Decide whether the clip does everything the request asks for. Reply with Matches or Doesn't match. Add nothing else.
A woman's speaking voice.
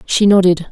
Matches